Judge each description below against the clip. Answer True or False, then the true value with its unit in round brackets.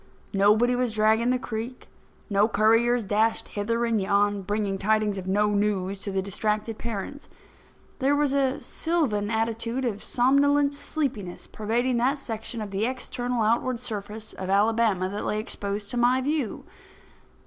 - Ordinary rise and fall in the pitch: True (3.2 semitones)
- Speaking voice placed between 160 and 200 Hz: False (220 Hz)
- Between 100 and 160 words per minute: True (150 wpm)